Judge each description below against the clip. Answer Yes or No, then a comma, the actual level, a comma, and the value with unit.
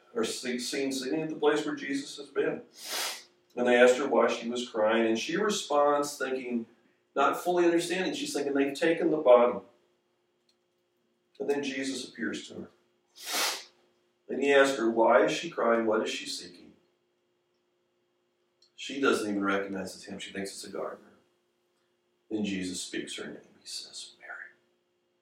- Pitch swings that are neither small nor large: No, wide, 6.3 semitones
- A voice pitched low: Yes, low, 125 Hz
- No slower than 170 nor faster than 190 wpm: No, average, 160 wpm